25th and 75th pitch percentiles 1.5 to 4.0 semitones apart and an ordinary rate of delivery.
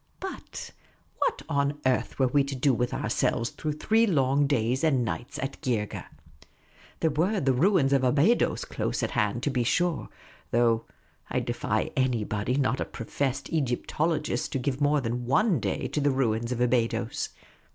Yes: average, 3.4 semitones; average, 170 wpm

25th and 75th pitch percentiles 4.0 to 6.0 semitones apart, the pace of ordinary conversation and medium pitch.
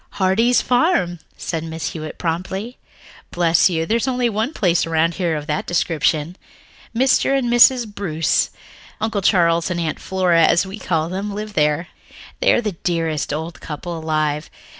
Yes: average, 4.6 semitones; average, 160 wpm; medium, 175 Hz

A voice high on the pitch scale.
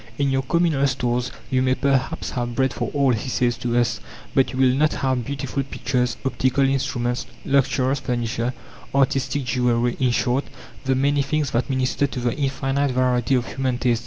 No: low, 130 Hz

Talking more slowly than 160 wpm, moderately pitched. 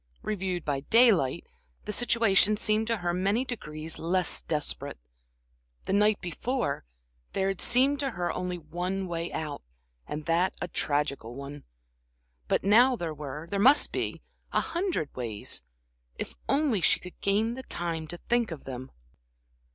Yes: average, 150 wpm; medium, 180 Hz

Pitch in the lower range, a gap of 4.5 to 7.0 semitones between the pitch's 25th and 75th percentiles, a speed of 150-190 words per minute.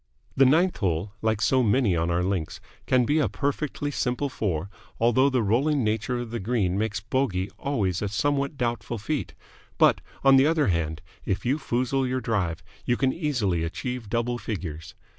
Yes: low, 115 Hz; wide, 5.5 semitones; average, 180 wpm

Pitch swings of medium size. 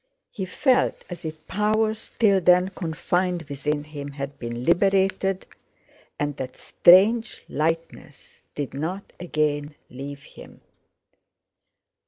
Yes: average, 4.8 semitones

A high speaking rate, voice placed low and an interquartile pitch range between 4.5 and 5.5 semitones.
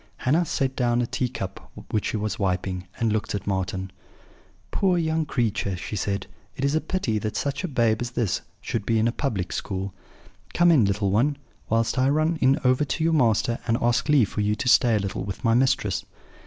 Yes: fast, 210 wpm; low, 115 Hz; average, 5.1 semitones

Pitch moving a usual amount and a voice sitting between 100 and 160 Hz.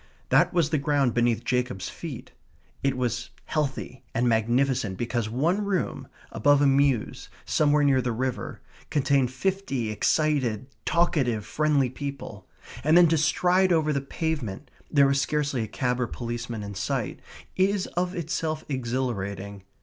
Yes: average, 4.4 semitones; low, 135 Hz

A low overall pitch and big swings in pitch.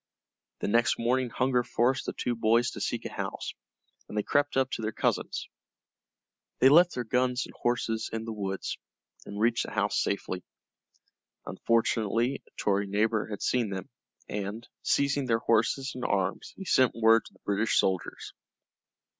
No: low, 115 Hz; average, 3.2 semitones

